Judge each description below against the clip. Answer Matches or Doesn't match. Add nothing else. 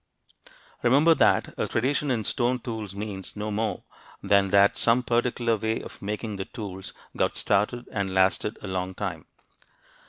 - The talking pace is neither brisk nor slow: Matches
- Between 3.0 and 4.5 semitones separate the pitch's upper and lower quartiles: Matches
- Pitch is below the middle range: Matches